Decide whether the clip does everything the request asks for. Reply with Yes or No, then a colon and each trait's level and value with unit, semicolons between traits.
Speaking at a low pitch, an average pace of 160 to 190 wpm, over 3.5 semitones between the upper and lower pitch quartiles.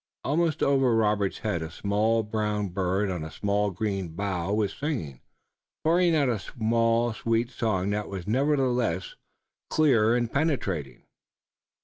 No: low, 110 Hz; slow, 135 wpm; average, 4.0 semitones